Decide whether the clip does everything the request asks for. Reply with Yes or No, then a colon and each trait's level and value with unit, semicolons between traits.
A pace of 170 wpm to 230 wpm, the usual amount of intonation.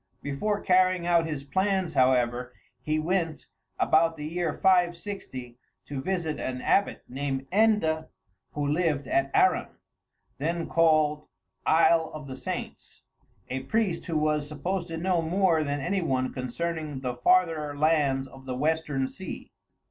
No: average, 140 wpm; average, 4.0 semitones